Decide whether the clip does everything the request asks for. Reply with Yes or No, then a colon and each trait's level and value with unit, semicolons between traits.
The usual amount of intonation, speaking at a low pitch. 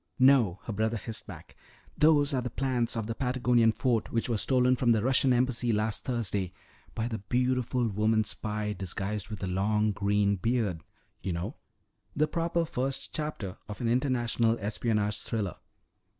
Yes: average, 3.3 semitones; low, 115 Hz